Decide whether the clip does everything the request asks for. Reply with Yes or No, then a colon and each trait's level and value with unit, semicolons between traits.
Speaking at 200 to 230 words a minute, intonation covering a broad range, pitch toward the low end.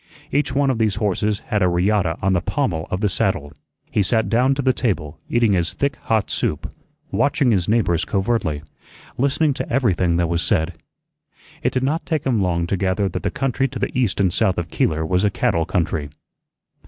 Yes: fast, 205 wpm; wide, 6.1 semitones; low, 100 Hz